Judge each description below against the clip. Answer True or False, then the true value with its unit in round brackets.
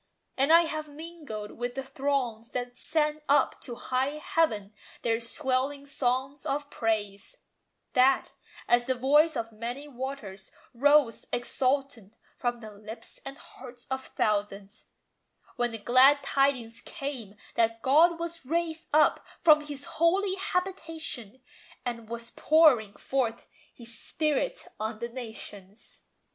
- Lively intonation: False (4.5 semitones)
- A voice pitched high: True (260 Hz)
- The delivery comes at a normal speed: False (130 wpm)